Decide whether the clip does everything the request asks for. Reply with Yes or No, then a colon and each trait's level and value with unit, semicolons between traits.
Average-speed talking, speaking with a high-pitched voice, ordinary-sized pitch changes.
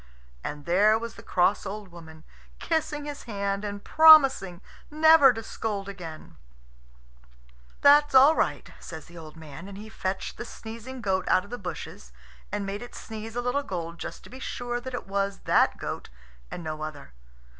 No: average, 180 wpm; high, 205 Hz; wide, 5.7 semitones